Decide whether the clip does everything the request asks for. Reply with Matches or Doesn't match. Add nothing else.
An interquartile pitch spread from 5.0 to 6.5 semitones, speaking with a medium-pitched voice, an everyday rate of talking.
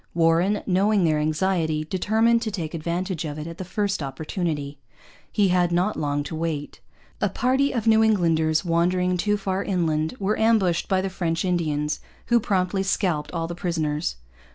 Doesn't match